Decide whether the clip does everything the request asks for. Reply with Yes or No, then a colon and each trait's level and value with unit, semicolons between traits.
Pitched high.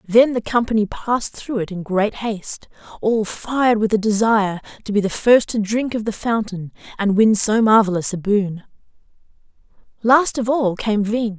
Yes: high, 215 Hz